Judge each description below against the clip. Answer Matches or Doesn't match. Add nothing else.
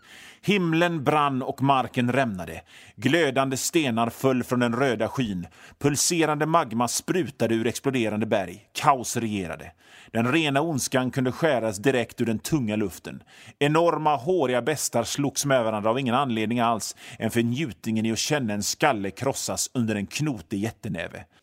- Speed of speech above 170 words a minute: Doesn't match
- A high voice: Doesn't match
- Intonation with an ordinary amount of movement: Matches